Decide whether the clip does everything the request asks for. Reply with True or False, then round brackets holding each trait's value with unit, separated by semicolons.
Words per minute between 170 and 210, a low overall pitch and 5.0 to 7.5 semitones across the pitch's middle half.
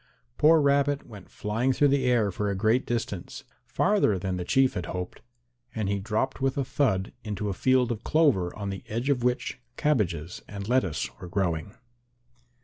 True (180 wpm; 110 Hz; 5.4 semitones)